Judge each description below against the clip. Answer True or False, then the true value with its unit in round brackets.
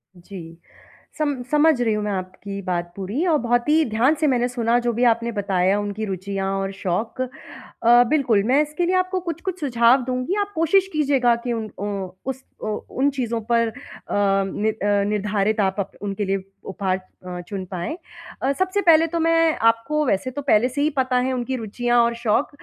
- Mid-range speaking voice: False (235 Hz)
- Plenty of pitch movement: True (5.9 semitones)